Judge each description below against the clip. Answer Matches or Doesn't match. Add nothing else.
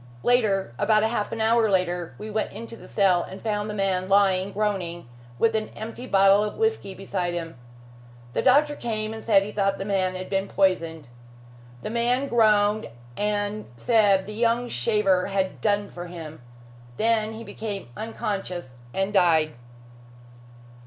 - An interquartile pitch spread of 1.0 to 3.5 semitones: Matches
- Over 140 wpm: Matches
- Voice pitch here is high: Matches